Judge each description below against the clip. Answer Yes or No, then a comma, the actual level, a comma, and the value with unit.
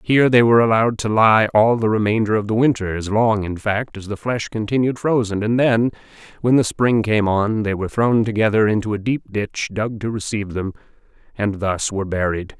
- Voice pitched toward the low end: Yes, low, 110 Hz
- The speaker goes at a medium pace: No, fast, 210 wpm